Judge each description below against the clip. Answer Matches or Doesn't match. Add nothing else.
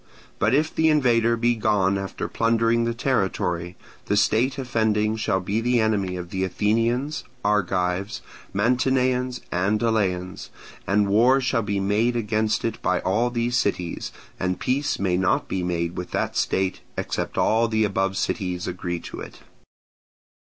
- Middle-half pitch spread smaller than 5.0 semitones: Matches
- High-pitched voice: Doesn't match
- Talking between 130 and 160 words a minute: Matches